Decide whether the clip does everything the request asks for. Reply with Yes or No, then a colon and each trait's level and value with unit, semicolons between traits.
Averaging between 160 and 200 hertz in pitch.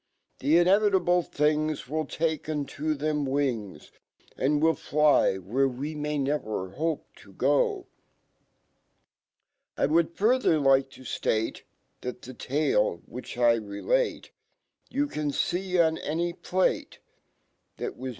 No: medium, 150 Hz